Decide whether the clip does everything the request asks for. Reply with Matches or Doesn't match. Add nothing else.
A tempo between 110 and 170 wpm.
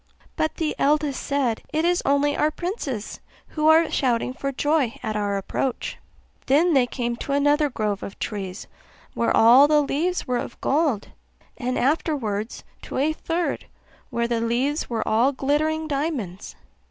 Matches